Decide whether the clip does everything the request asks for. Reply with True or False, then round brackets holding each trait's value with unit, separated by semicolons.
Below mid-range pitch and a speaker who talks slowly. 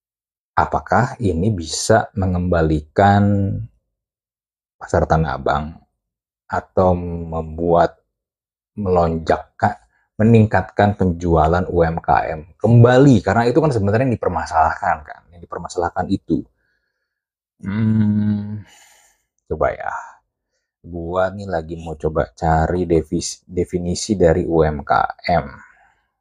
True (90 Hz; 80 wpm)